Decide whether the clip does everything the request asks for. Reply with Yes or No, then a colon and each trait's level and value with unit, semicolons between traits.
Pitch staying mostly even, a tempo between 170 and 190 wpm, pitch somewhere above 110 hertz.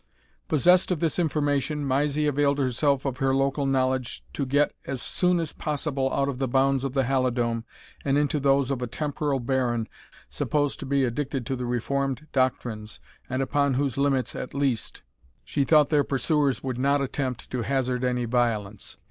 Yes: narrow, 2.1 semitones; average, 175 wpm; low, 135 Hz